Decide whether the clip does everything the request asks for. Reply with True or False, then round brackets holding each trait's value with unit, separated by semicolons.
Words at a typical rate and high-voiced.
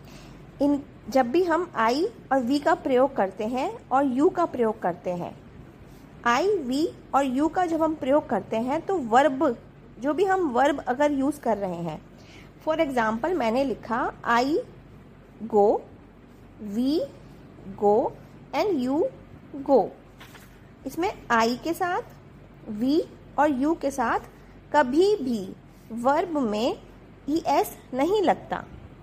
True (135 wpm; 275 Hz)